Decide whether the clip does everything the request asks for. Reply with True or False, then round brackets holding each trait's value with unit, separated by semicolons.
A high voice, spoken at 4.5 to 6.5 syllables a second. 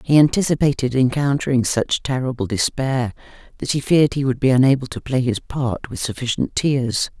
False (130 Hz; 5.3 syllables/s)